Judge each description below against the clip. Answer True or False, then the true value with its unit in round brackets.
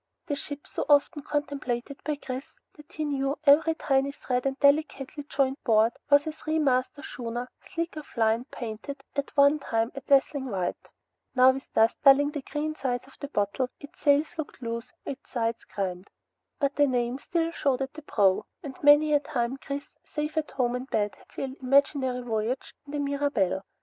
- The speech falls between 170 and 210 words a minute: True (185 wpm)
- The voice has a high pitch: True (275 Hz)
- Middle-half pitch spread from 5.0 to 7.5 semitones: False (3.0 semitones)